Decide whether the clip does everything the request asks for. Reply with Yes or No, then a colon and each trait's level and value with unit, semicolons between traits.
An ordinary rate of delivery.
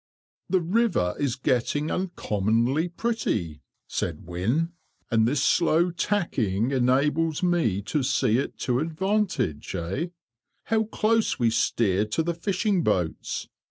No: slow, 125 wpm